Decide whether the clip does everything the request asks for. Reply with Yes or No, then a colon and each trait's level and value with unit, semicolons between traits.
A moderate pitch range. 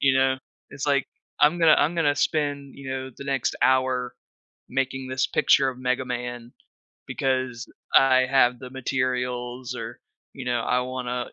No: narrow, 1.4 semitones